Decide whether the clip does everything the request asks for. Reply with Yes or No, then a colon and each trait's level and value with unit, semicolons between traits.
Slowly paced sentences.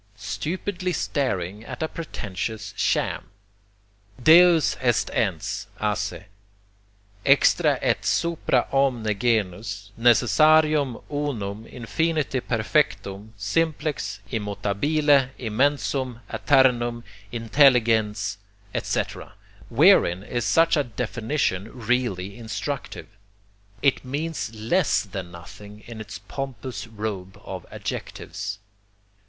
Yes: slow, 90 wpm